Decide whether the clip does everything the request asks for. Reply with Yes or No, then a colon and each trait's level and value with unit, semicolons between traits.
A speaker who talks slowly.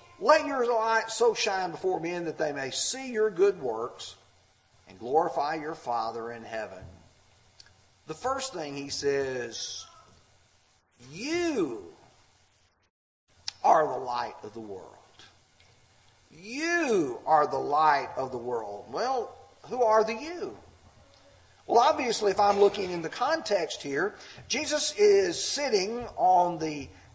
Yes: slow, 130 wpm